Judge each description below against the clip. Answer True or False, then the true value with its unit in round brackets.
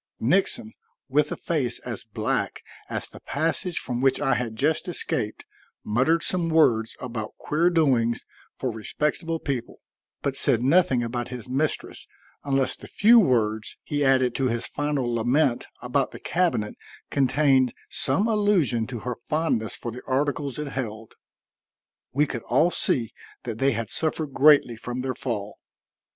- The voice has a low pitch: True (130 Hz)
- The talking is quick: False (150 wpm)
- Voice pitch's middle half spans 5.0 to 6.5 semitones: False (4.3 semitones)